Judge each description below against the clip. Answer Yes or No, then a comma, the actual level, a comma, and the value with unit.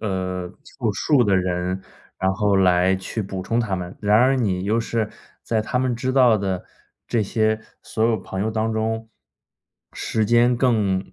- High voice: No, low, 110 Hz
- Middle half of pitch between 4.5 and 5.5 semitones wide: No, average, 3.4 semitones